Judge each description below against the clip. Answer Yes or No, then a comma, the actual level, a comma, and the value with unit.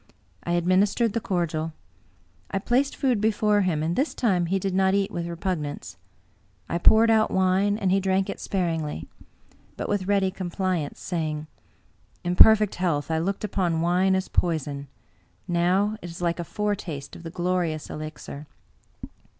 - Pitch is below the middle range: No, medium, 185 Hz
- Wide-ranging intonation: No, average, 3.0 semitones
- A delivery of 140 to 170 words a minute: Yes, average, 160 wpm